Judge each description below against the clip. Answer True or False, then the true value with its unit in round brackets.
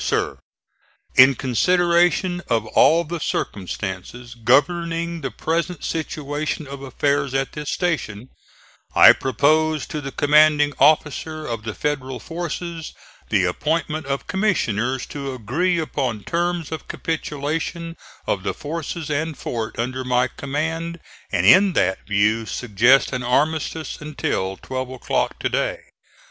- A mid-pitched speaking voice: True (145 Hz)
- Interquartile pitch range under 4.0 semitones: False (4.6 semitones)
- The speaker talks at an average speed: False (130 wpm)